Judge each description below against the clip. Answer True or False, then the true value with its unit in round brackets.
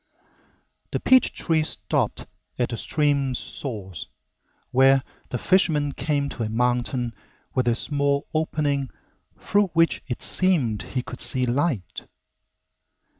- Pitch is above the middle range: False (135 Hz)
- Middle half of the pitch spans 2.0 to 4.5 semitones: True (3.7 semitones)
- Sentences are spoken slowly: True (125 wpm)